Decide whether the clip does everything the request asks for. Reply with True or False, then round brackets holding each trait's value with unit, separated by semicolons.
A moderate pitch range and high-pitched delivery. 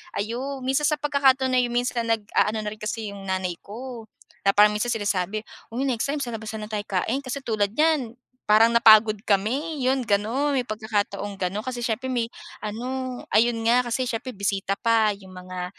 True (3.6 semitones; 225 Hz)